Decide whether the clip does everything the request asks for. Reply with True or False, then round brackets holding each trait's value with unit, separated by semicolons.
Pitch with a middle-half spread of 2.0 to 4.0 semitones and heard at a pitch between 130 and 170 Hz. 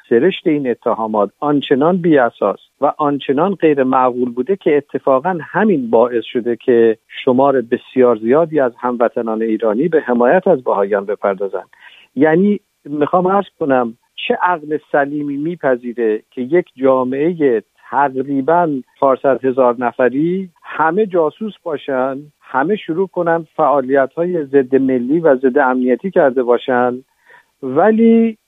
False (5.0 semitones; 140 Hz)